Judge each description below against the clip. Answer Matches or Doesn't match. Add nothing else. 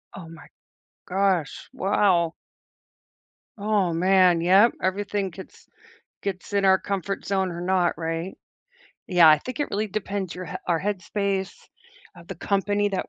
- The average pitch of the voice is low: Doesn't match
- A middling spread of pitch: Doesn't match